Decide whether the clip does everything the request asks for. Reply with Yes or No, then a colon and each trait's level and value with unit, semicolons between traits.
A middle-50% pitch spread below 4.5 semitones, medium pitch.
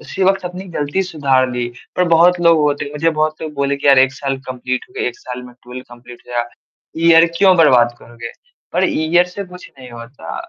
No: average, 5.1 semitones; medium, 145 Hz